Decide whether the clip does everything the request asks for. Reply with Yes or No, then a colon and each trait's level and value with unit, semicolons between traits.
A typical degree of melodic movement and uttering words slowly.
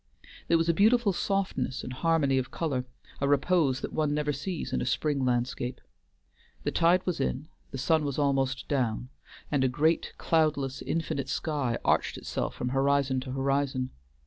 No: average, 3.5 semitones; average, 170 wpm